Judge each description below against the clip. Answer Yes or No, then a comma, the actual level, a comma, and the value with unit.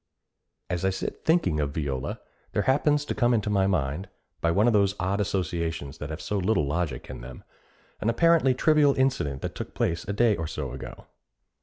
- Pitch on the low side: Yes, very low, 95 Hz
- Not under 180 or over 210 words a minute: Yes, average, 195 wpm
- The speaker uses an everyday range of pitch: No, wide, 7.4 semitones